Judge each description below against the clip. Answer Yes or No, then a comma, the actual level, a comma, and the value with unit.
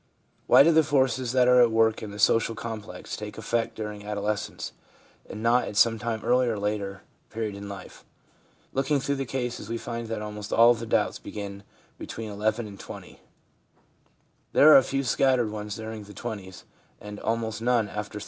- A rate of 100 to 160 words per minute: No, average, 185 wpm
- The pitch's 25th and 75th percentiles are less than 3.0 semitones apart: Yes, narrow, 2.6 semitones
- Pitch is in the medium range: No, low, 110 Hz